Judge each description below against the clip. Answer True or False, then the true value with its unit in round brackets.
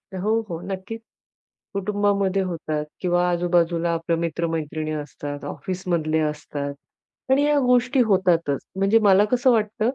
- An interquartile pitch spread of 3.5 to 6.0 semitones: True (4.1 semitones)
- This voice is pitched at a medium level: True (180 Hz)